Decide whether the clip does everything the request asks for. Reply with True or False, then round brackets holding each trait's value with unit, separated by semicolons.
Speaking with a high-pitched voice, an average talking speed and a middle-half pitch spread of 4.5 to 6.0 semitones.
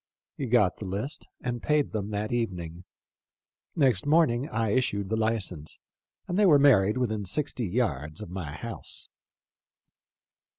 False (110 Hz; 145 wpm; 5.1 semitones)